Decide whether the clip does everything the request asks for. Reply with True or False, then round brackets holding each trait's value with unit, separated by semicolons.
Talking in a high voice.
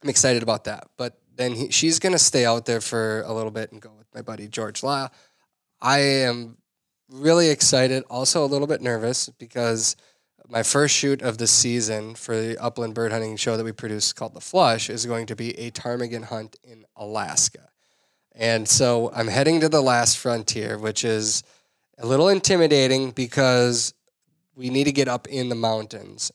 False (120 Hz)